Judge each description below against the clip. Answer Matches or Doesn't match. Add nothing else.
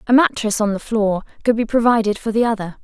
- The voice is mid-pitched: Doesn't match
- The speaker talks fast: Matches